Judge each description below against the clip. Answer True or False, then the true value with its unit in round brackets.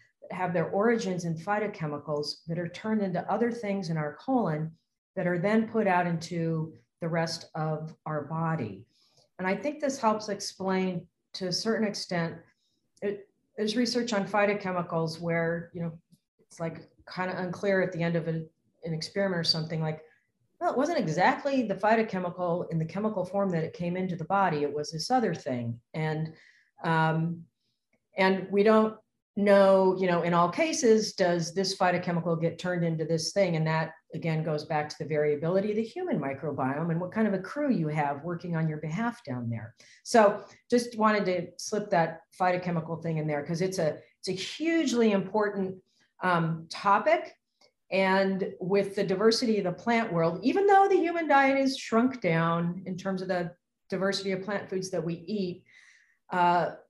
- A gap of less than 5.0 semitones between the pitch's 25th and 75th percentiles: True (3.9 semitones)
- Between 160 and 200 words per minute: True (180 wpm)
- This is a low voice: False (180 Hz)